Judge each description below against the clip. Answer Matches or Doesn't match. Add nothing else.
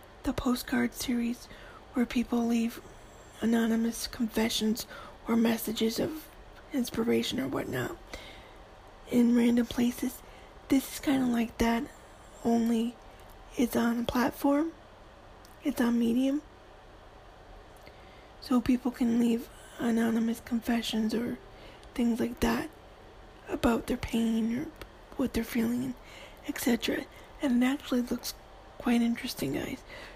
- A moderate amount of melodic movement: Doesn't match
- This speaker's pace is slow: Matches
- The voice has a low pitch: Doesn't match